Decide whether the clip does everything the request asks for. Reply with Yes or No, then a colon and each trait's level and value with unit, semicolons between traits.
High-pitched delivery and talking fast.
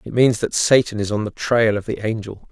No: low, 110 Hz; fast, 260 wpm